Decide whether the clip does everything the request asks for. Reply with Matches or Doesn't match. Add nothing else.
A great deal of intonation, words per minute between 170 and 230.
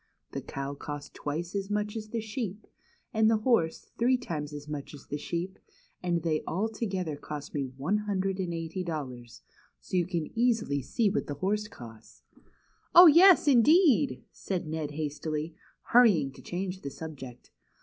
Matches